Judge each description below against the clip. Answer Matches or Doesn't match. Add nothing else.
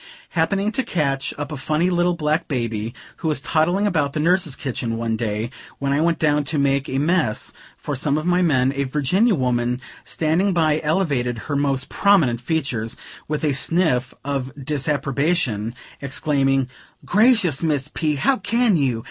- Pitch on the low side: Doesn't match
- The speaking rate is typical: Matches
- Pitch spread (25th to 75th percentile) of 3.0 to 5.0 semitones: Matches